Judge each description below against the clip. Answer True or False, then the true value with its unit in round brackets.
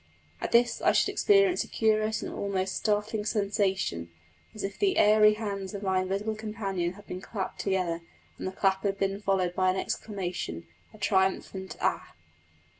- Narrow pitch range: True (2.1 semitones)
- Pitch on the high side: True (195 Hz)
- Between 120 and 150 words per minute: False (170 wpm)